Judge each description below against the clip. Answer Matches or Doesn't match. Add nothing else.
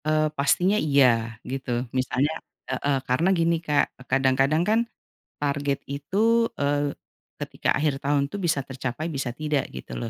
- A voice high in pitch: Doesn't match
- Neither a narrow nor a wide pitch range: Doesn't match